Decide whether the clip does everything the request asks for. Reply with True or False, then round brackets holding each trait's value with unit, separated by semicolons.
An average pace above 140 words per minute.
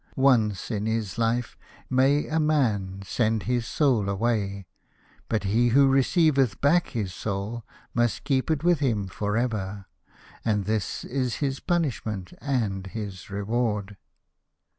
False (135 wpm)